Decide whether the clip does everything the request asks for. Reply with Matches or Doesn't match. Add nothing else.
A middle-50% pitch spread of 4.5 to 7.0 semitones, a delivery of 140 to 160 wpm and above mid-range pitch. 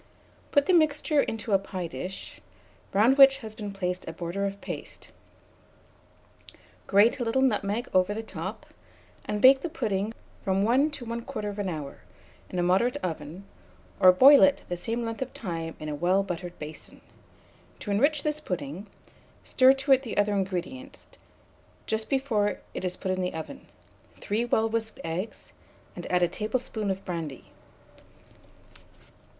Matches